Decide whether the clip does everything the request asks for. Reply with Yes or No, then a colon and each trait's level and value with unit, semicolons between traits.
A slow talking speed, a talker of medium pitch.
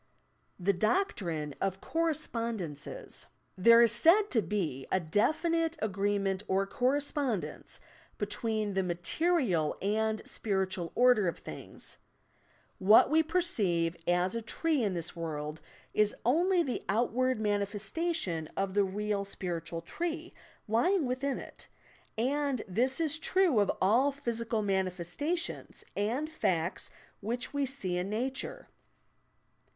No: slow, 125 wpm; high, 215 Hz